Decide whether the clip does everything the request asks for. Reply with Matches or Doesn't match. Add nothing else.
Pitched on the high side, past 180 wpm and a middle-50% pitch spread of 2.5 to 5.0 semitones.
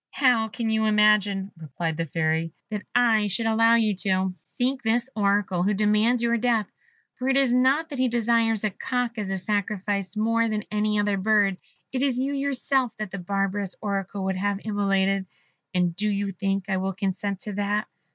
Matches